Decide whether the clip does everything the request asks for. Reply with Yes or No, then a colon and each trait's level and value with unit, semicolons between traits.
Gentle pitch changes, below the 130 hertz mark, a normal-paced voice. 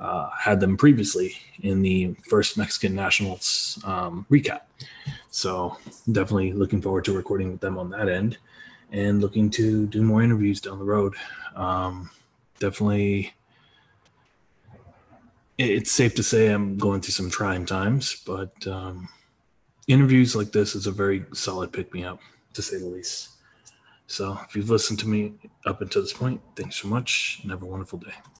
Yes: narrow, 2.2 semitones; low, 100 Hz; average, 165 wpm